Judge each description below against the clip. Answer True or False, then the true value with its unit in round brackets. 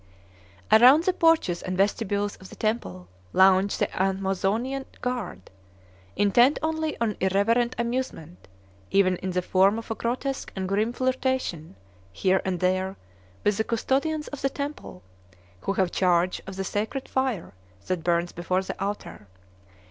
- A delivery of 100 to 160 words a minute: True (145 wpm)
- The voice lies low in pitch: False (200 Hz)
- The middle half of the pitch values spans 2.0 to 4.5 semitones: False (5.2 semitones)